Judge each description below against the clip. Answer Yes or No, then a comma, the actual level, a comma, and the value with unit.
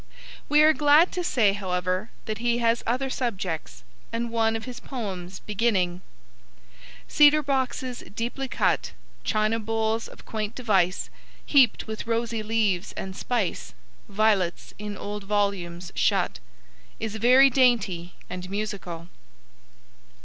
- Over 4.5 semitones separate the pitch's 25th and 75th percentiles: No, average, 3.9 semitones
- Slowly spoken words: Yes, slow, 125 wpm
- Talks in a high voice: Yes, high, 220 Hz